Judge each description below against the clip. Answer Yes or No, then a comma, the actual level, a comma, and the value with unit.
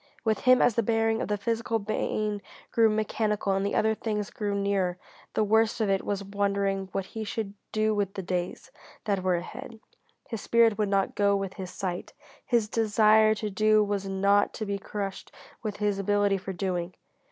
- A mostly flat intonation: Yes, narrow, 1.8 semitones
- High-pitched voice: Yes, high, 205 Hz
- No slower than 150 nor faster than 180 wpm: No, average, 190 wpm